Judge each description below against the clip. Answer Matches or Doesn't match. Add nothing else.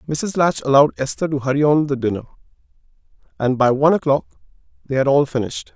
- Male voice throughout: Matches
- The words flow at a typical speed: Matches